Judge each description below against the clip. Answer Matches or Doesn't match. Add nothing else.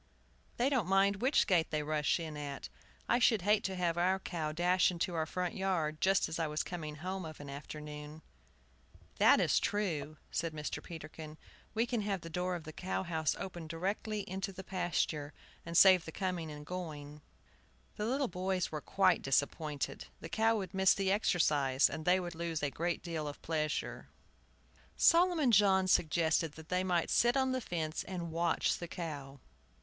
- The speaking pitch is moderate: Matches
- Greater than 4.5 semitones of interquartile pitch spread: Doesn't match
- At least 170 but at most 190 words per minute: Matches